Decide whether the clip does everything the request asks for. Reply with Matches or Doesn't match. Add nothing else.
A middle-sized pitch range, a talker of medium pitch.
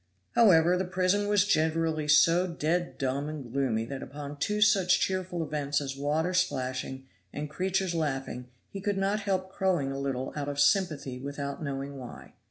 Matches